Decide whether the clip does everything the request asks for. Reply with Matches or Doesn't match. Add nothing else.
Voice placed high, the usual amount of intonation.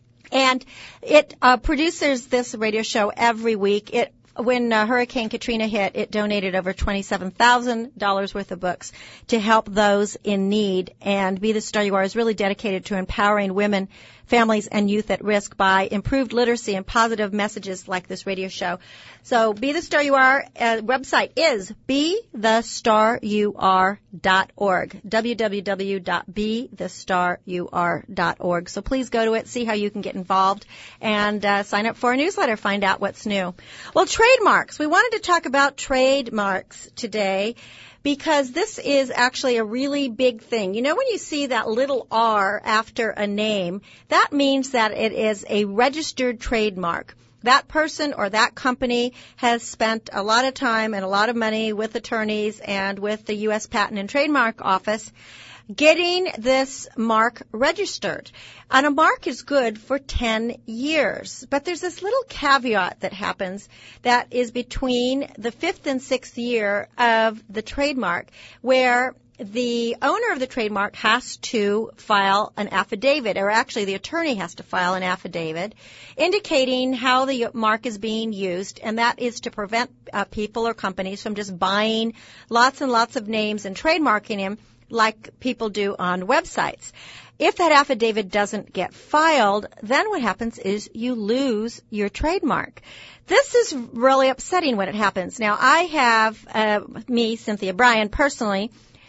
Matches